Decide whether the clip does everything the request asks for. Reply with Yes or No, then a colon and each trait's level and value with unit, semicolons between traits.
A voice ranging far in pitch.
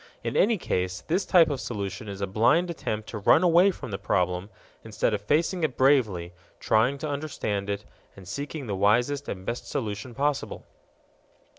Yes: wide, 6.7 semitones